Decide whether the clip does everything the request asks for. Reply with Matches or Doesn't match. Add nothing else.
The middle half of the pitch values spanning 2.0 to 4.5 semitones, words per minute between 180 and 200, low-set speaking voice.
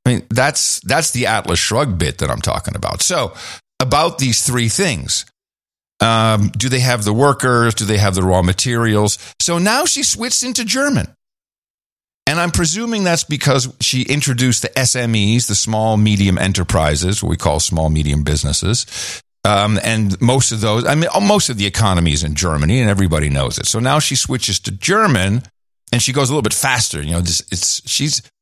Doesn't match